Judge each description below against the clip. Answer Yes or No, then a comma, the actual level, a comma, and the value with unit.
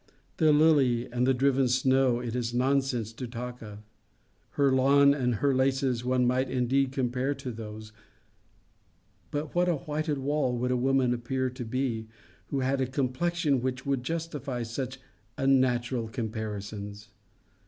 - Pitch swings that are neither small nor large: No, narrow, 2.1 semitones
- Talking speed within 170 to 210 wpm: No, average, 150 wpm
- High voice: No, low, 130 Hz